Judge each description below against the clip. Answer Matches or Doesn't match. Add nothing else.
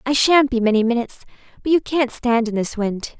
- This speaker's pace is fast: Matches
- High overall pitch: Matches